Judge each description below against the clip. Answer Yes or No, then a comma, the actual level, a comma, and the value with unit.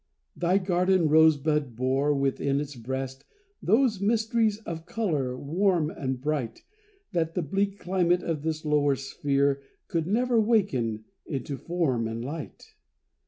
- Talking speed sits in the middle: No, slow, 130 wpm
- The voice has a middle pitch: Yes, medium, 155 Hz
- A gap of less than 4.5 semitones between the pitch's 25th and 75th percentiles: No, average, 5.2 semitones